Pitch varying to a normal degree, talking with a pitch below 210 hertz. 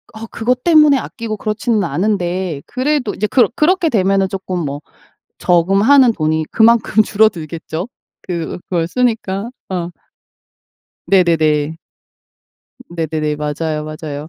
No: wide, 6.0 semitones; high, 190 Hz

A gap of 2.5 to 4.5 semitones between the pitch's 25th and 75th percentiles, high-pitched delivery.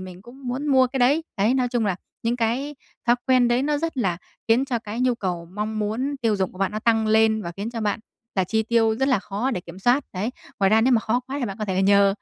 Yes: average, 3.7 semitones; high, 225 Hz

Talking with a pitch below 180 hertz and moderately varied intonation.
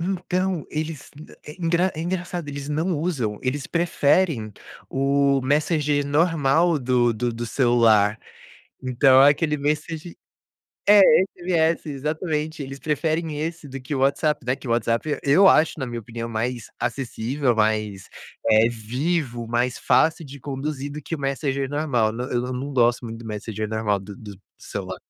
Yes: medium, 140 Hz; average, 4.7 semitones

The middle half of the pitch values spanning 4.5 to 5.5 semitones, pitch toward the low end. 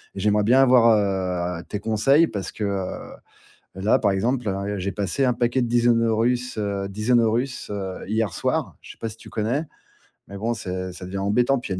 No: average, 3.5 semitones; low, 105 Hz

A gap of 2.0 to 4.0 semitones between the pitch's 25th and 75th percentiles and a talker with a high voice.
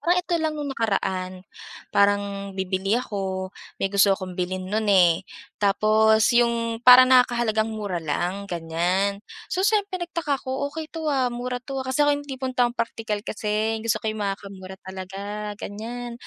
No: average, 4.4 semitones; high, 215 Hz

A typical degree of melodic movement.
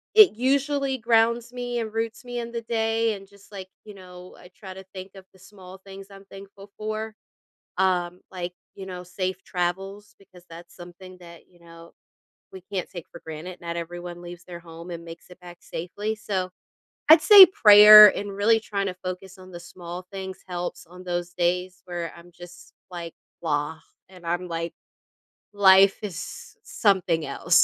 Yes: average, 3.0 semitones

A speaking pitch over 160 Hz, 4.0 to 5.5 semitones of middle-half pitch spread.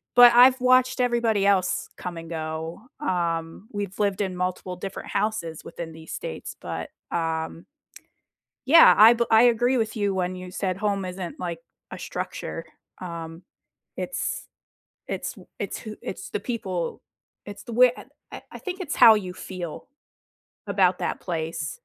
Yes: high, 190 Hz; average, 4.9 semitones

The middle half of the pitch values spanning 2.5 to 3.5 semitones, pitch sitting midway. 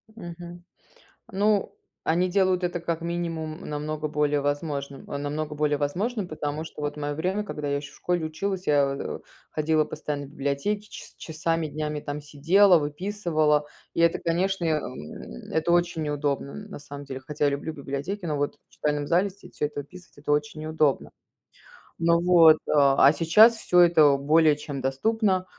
Yes: average, 3.2 semitones; medium, 155 Hz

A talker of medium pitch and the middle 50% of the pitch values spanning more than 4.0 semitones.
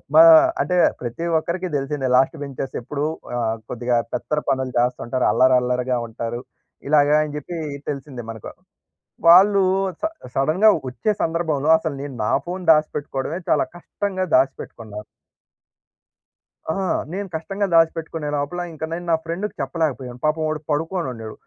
Yes: medium, 150 Hz; average, 4.7 semitones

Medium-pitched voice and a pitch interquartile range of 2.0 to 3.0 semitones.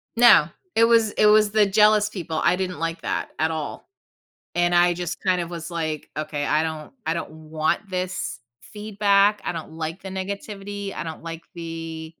No: medium, 175 Hz; average, 3.9 semitones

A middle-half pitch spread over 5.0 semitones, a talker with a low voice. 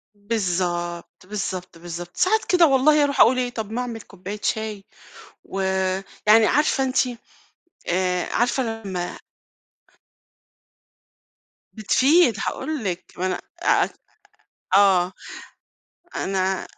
No: wide, 5.5 semitones; high, 205 Hz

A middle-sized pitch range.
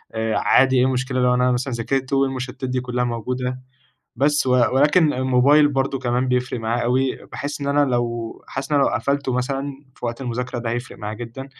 No: narrow, 1.7 semitones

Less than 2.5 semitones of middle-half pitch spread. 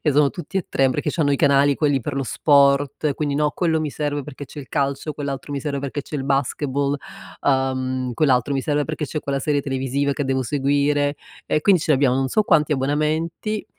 Yes: narrow, 1.7 semitones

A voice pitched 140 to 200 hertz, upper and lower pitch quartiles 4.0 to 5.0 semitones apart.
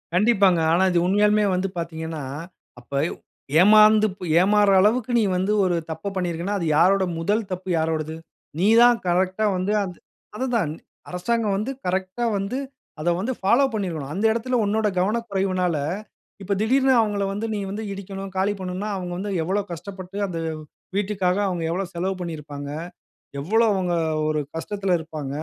No: high, 190 Hz; average, 3.0 semitones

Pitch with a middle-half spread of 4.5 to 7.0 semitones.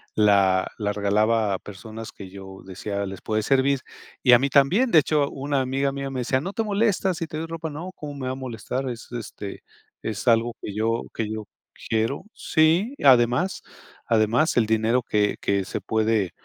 Yes: average, 4.8 semitones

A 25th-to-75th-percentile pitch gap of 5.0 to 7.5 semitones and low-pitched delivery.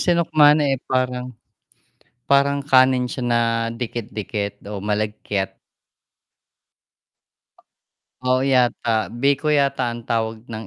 No: average, 3.8 semitones; low, 125 Hz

